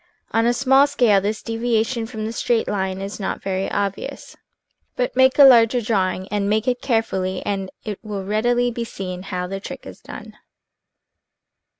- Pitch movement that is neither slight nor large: Yes, average, 3.7 semitones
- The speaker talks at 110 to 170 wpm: No, average, 180 wpm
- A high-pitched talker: Yes, high, 215 Hz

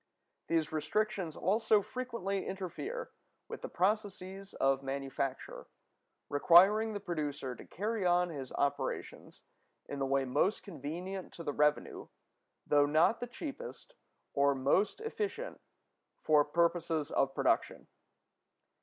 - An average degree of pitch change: No, wide, 6.2 semitones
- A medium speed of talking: No, slow, 120 wpm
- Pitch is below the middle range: No, medium, 175 Hz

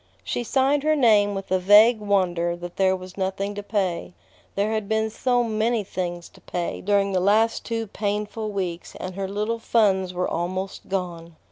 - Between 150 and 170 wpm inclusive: No, average, 180 wpm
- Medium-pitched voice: No, high, 200 Hz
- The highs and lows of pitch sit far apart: No, average, 2.9 semitones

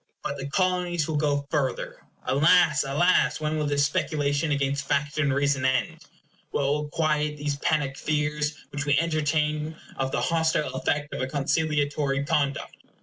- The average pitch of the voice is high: No, medium, 145 Hz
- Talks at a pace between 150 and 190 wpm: Yes, average, 155 wpm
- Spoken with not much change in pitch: Yes, narrow, 1.5 semitones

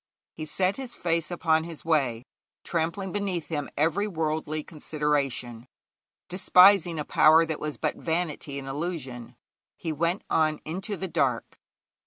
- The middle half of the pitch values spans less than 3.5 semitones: Yes, average, 2.9 semitones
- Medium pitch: Yes, medium, 160 Hz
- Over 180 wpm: No, average, 140 wpm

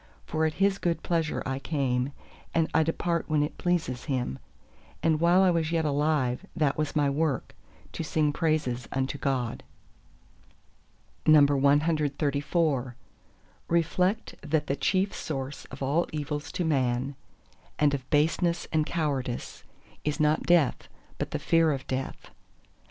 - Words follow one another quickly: No, average, 140 wpm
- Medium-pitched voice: Yes, medium, 150 Hz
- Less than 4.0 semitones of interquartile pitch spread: Yes, average, 3.1 semitones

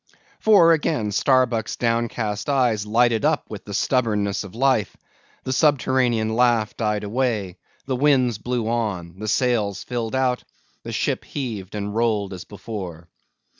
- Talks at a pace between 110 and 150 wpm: Yes, average, 140 wpm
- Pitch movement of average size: Yes, average, 3.5 semitones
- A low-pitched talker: Yes, low, 115 Hz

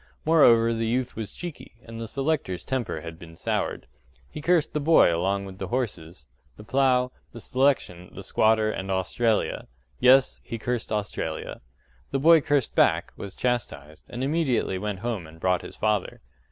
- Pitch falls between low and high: No, low, 115 Hz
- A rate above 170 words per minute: No, average, 165 wpm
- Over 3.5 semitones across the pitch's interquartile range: Yes, wide, 5.6 semitones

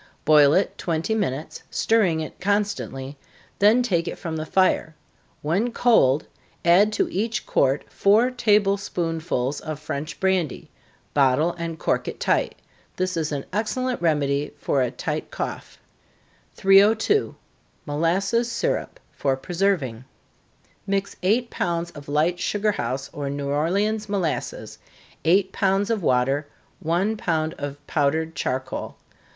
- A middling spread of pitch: No, wide, 5.7 semitones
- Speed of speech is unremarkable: No, slow, 130 wpm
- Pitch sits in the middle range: Yes, medium, 170 Hz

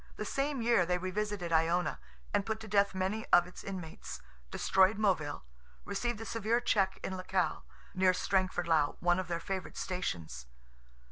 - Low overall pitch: No, medium, 185 Hz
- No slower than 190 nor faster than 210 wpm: No, average, 160 wpm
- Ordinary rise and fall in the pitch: Yes, average, 3.1 semitones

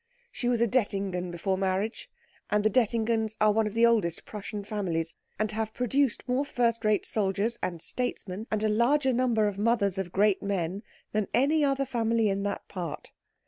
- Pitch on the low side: No, high, 215 Hz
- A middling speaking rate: Yes, average, 185 wpm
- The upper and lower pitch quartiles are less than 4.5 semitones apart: Yes, average, 3.0 semitones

